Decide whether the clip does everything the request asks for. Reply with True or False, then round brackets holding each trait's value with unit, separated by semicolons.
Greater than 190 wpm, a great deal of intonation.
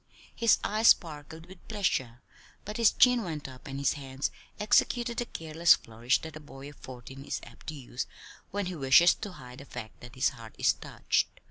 True (200 wpm; 6.2 semitones)